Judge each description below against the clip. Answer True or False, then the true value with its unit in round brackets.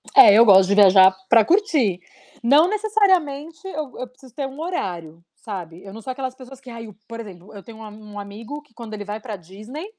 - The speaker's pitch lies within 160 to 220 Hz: False (230 Hz)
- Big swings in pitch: True (5.9 semitones)